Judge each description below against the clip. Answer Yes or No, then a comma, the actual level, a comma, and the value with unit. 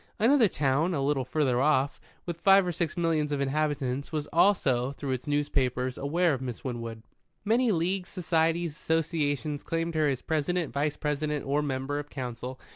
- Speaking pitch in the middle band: Yes, medium, 150 Hz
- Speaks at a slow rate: No, average, 170 wpm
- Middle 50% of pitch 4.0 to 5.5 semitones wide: No, average, 3.6 semitones